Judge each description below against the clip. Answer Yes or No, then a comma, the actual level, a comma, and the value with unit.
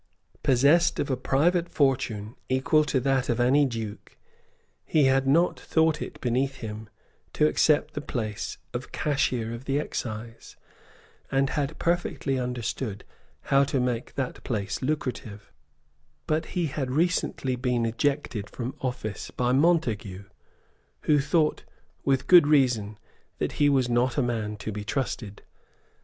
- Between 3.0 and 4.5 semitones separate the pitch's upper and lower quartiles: Yes, average, 3.8 semitones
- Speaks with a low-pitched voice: Yes, low, 130 Hz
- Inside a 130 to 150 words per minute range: Yes, average, 140 wpm